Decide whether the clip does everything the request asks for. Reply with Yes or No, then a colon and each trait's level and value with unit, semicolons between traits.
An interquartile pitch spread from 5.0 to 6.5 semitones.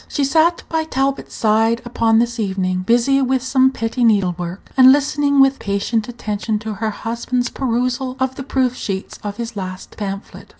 No: average, 3.9 semitones